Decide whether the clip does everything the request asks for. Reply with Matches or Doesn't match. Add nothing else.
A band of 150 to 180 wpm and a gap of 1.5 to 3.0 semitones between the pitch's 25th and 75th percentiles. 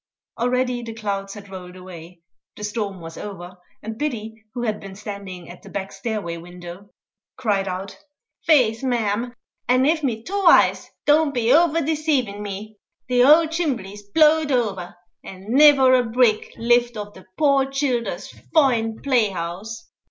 Doesn't match